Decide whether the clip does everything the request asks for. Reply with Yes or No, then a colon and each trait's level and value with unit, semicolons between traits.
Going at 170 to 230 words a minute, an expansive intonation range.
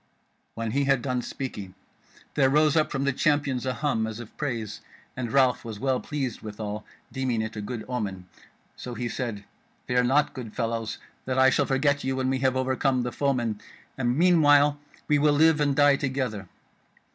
No: average, 185 wpm; average, 3.5 semitones